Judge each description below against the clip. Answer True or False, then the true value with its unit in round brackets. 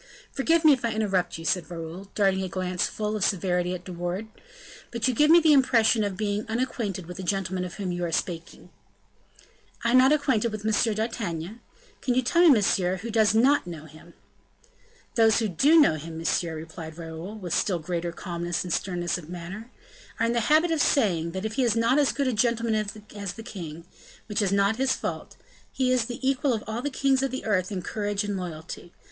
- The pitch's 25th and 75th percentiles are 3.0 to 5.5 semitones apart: True (5.0 semitones)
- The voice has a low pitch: False (205 Hz)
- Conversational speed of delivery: False (215 wpm)